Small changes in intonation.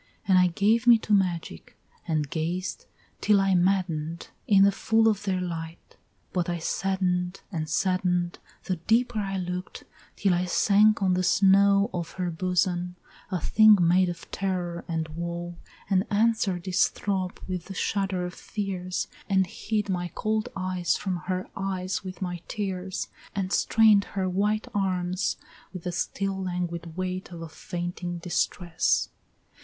Yes: narrow, 2.0 semitones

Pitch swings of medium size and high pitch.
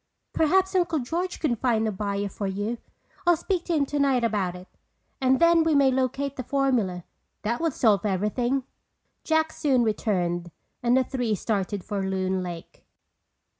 No: wide, 5.9 semitones; high, 240 Hz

